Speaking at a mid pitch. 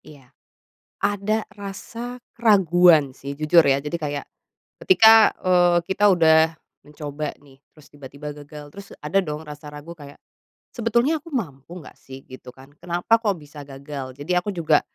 Yes: medium, 160 Hz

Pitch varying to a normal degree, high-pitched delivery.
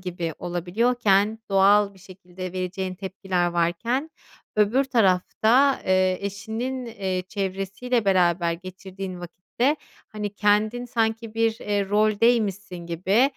Yes: average, 3.4 semitones; high, 200 Hz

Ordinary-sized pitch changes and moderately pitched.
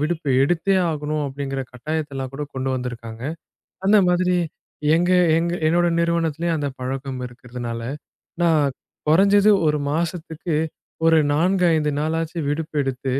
Yes: average, 4.0 semitones; medium, 155 Hz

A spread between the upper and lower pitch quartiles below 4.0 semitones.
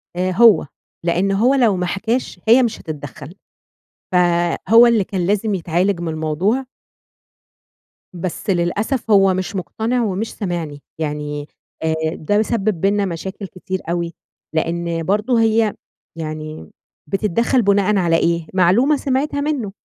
No: average, 4.6 semitones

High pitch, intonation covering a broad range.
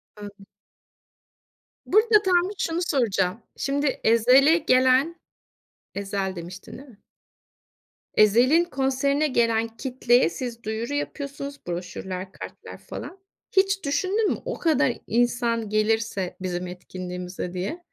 Yes: high, 240 Hz; wide, 6.4 semitones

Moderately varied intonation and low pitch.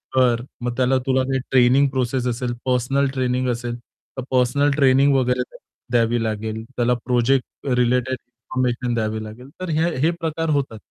No: narrow, 1.7 semitones; low, 125 Hz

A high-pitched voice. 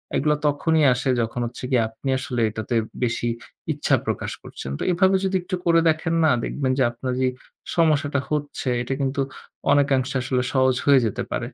No: low, 135 Hz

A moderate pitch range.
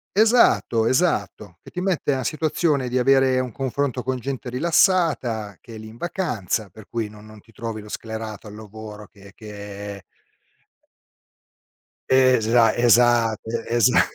Yes: average, 3.6 semitones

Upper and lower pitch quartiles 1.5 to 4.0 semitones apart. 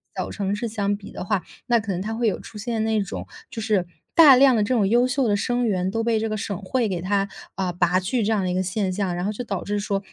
Yes: average, 2.8 semitones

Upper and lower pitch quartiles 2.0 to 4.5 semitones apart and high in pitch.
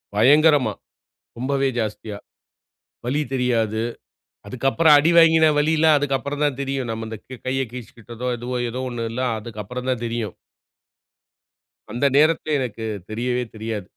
No: average, 3.9 semitones; low, 125 Hz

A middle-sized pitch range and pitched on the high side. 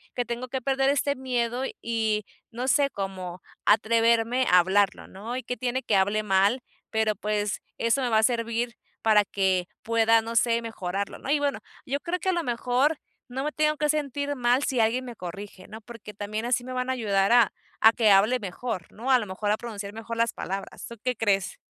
Yes: average, 3.6 semitones; high, 230 Hz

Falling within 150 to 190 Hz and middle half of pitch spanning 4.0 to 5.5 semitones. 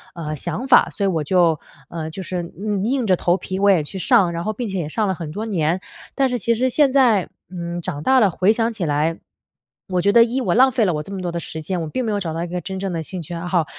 Yes: medium, 185 Hz; average, 4.6 semitones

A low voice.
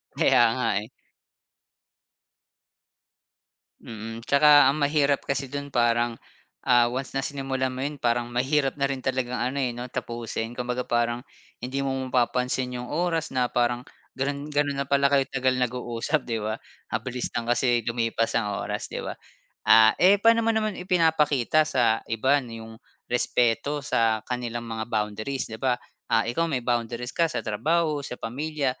Yes: low, 125 Hz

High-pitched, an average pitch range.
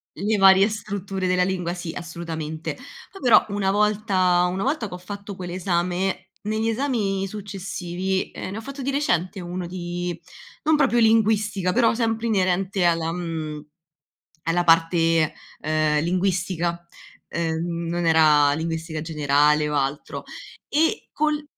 No: medium, 180 Hz; average, 3.8 semitones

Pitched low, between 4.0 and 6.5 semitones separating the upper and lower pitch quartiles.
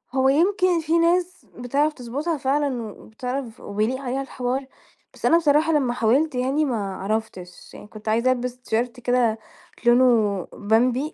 No: very high, 250 Hz; average, 4.3 semitones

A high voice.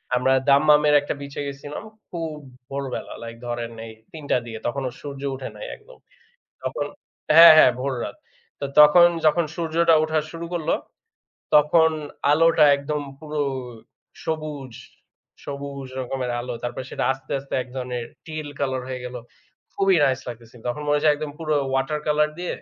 No: medium, 145 Hz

